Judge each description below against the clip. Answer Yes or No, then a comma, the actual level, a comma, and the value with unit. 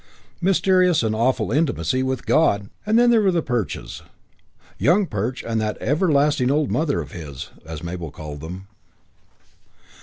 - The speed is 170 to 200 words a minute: No, average, 155 wpm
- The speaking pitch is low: Yes, low, 125 Hz